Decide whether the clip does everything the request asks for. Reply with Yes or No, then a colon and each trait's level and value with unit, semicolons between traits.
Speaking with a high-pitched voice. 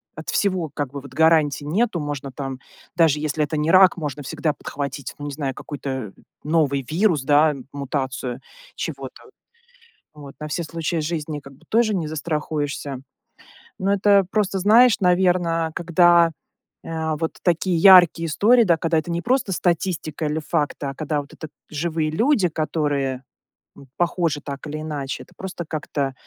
No: medium, 155 Hz